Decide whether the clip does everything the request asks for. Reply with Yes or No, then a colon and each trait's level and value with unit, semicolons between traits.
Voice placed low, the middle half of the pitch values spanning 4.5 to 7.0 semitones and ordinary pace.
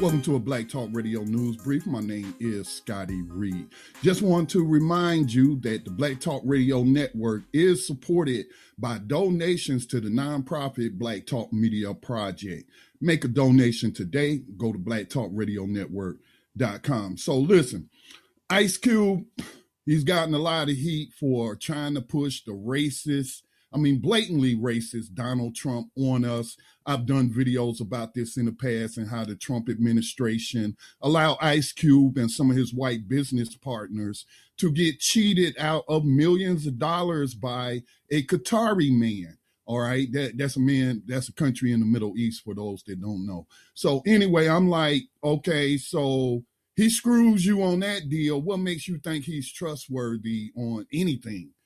Yes: low, 130 Hz; average, 5.0 semitones; average, 160 wpm